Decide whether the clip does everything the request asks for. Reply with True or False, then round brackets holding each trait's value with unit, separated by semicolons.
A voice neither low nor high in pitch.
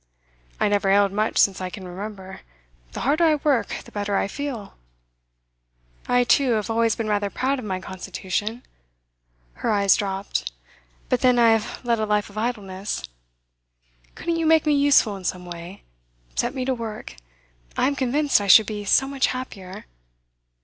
False (215 Hz)